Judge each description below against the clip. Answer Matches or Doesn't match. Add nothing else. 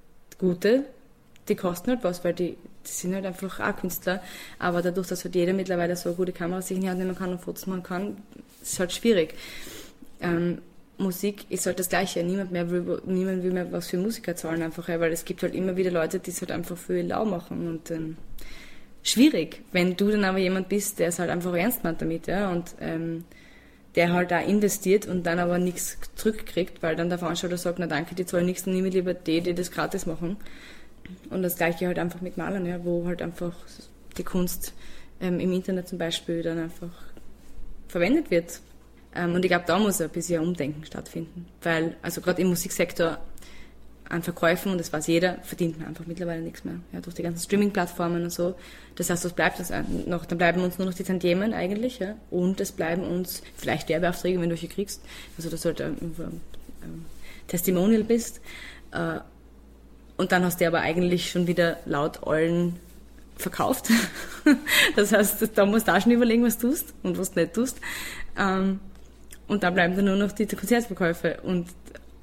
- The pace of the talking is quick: Matches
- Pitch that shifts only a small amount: Matches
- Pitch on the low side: Doesn't match